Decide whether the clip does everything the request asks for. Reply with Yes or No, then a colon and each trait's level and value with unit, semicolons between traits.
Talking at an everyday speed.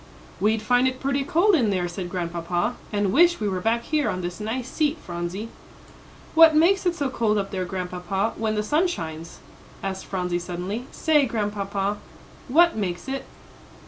Yes: average, 175 wpm